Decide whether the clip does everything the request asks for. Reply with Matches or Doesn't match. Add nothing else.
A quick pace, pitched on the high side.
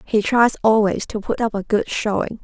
Matches